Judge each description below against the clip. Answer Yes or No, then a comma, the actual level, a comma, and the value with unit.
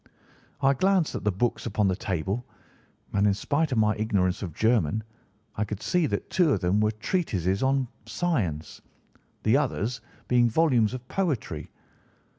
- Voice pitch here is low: Yes, low, 110 Hz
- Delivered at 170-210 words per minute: No, average, 160 wpm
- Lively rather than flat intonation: Yes, wide, 5.7 semitones